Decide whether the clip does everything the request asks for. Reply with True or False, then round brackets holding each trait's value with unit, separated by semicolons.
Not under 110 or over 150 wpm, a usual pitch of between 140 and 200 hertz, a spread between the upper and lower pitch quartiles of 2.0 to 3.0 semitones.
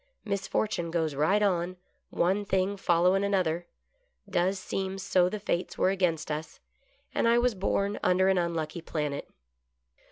True (140 wpm; 185 Hz; 2.7 semitones)